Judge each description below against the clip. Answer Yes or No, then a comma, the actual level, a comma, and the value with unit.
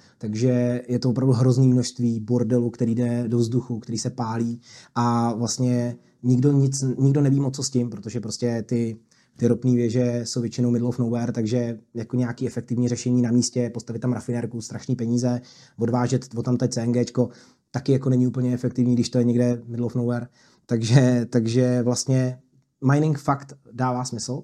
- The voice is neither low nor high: No, low, 120 Hz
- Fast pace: Yes, fast, 175 wpm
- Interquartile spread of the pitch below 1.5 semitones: Yes, narrow, 1.0 semitones